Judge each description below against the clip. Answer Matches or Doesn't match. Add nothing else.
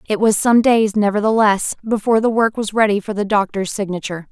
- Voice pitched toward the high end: Matches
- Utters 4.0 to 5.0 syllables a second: Doesn't match